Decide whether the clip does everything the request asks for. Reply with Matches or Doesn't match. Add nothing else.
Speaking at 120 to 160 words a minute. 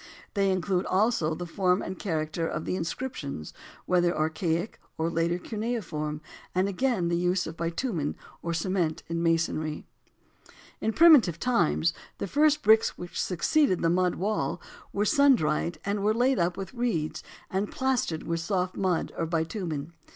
Matches